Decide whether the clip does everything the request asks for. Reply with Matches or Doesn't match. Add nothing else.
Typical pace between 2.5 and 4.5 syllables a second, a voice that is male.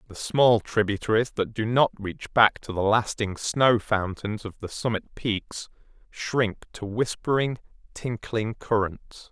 Matches